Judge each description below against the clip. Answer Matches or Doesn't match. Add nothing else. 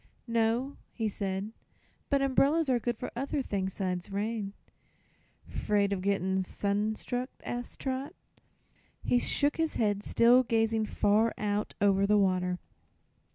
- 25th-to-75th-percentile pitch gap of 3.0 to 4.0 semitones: Matches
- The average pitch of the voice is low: Doesn't match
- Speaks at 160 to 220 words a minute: Doesn't match